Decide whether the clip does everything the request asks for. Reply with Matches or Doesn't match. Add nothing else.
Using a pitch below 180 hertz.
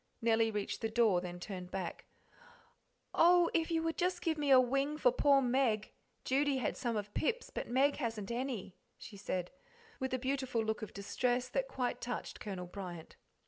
Doesn't match